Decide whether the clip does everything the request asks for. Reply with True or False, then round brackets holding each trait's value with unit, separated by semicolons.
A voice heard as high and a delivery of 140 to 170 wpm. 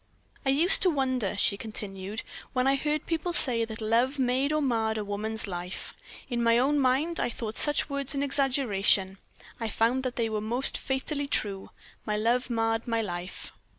False (235 Hz; 185 wpm)